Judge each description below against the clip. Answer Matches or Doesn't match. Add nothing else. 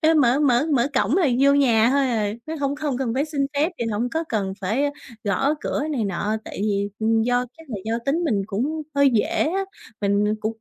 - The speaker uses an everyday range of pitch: Matches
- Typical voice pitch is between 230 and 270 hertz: Matches